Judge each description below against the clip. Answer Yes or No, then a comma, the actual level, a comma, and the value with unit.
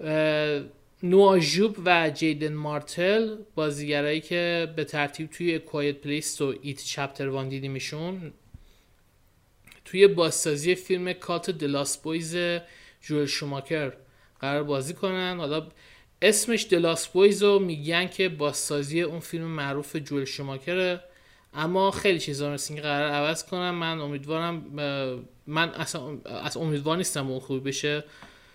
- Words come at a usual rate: Yes, average, 120 wpm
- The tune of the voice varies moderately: Yes, average, 3.3 semitones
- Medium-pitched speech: Yes, medium, 155 Hz